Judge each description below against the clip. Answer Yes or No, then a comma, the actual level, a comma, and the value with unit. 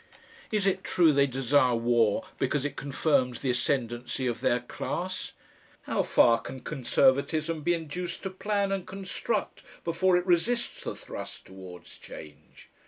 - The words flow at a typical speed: Yes, average, 145 wpm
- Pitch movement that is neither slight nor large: No, wide, 6.7 semitones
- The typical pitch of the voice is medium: Yes, medium, 145 Hz